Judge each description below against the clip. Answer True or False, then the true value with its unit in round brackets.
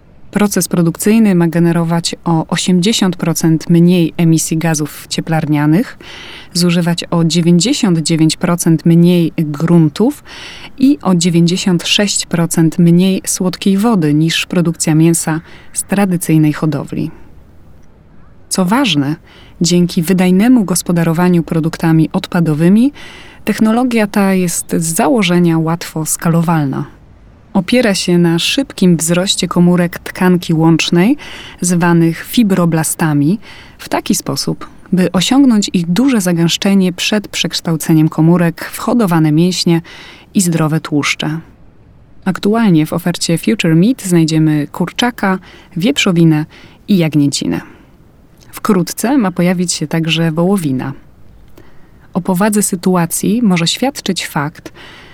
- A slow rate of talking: True (100 wpm)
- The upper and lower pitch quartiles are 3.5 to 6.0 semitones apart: False (2.9 semitones)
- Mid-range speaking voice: True (175 Hz)